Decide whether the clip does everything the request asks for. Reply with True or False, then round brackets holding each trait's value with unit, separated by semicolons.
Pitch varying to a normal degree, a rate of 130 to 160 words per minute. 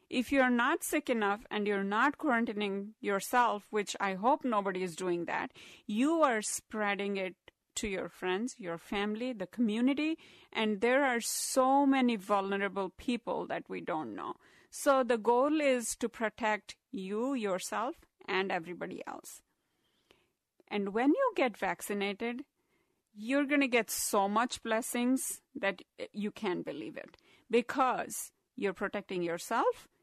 True (4.5 semitones; 140 wpm)